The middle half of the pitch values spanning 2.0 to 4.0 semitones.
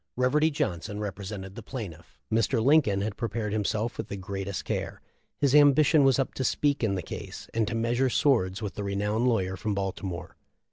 No: average, 4.5 semitones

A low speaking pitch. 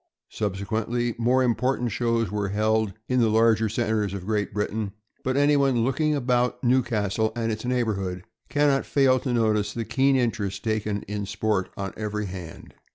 Yes: low, 110 Hz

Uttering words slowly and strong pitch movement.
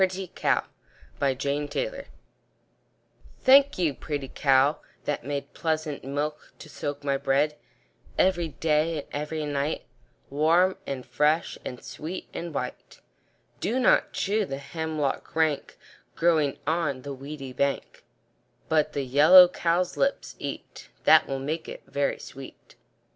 No: slow, 125 wpm; average, 3.1 semitones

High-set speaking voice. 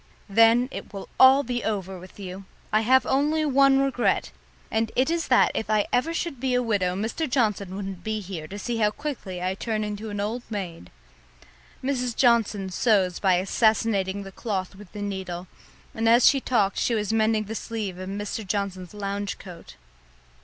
Yes: high, 210 Hz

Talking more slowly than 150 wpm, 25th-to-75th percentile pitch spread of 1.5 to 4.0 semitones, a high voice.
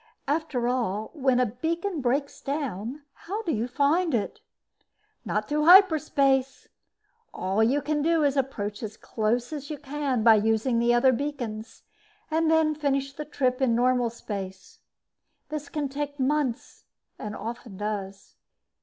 No: average, 140 wpm; average, 4.4 semitones; very high, 265 Hz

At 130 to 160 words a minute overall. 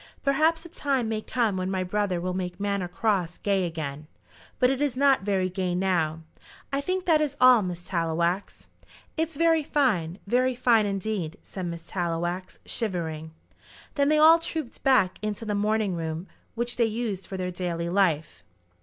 No: average, 170 wpm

